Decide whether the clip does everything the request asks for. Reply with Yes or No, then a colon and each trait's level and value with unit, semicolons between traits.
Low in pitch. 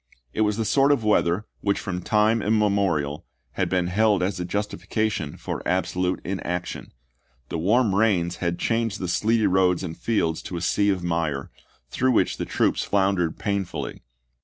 Yes: very low, 95 Hz